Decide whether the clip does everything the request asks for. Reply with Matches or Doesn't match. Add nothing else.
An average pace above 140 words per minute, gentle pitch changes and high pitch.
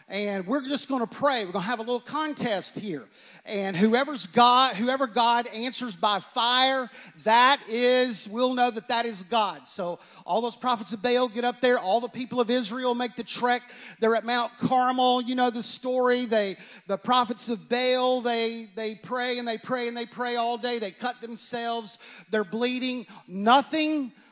Matches